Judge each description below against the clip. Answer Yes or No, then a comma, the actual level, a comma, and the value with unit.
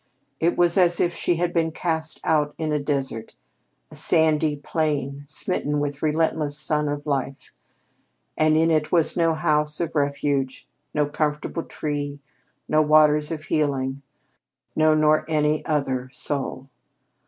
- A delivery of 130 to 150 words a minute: Yes, average, 145 wpm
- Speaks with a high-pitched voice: No, medium, 150 Hz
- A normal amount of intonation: No, narrow, 1.7 semitones